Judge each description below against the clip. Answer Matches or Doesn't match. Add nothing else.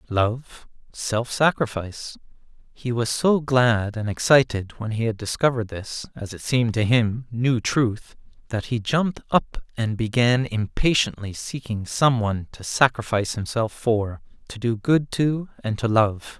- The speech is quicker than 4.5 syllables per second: Doesn't match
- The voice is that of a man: Matches